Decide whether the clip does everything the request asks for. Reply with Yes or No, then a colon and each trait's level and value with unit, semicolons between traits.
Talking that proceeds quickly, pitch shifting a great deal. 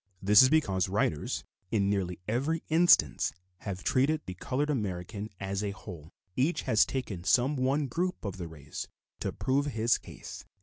No: average, 165 wpm; wide, 6.3 semitones